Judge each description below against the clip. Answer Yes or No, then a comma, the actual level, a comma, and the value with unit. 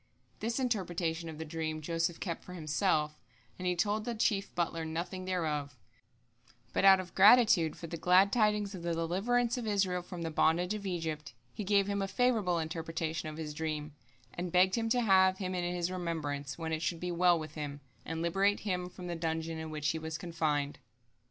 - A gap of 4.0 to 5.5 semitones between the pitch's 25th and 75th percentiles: No, average, 3.3 semitones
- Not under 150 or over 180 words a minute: No, average, 200 wpm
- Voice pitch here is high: No, medium, 175 Hz